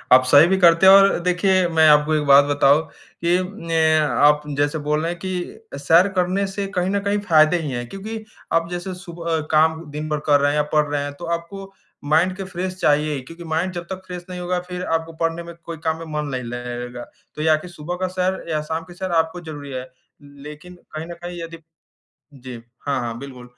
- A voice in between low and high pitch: Yes, medium, 165 Hz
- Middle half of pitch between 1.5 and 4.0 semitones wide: Yes, average, 3.4 semitones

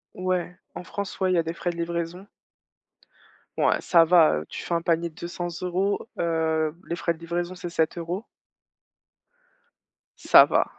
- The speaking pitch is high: No, medium, 170 Hz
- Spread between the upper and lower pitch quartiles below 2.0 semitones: Yes, narrow, 1.4 semitones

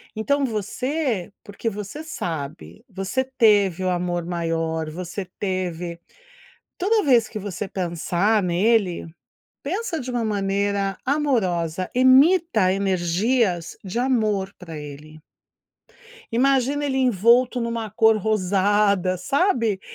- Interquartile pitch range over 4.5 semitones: Yes, wide, 5.6 semitones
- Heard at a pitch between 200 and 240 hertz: Yes, high, 205 Hz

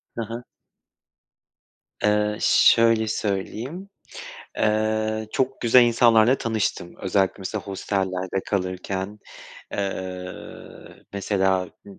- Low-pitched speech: Yes, low, 105 Hz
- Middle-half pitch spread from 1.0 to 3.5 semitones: Yes, average, 2.9 semitones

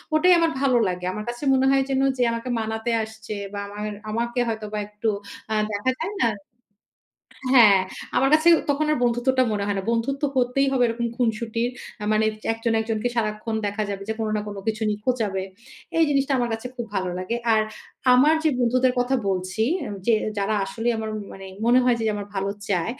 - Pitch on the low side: No, high, 230 Hz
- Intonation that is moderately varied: Yes, average, 3.0 semitones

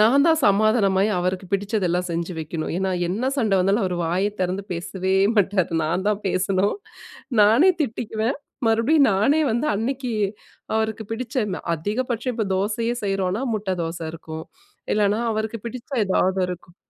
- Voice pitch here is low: No, high, 205 Hz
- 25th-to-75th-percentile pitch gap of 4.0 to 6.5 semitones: No, average, 3.6 semitones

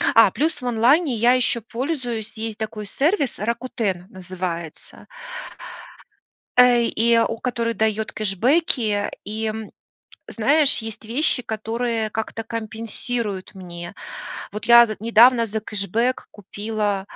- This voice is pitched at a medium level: No, high, 225 Hz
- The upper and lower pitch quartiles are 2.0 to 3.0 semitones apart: Yes, narrow, 2.4 semitones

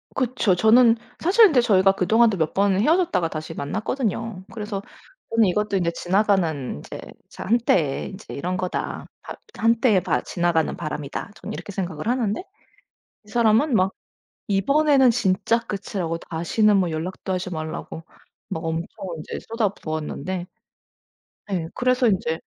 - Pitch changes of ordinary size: Yes, average, 5.0 semitones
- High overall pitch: Yes, high, 195 Hz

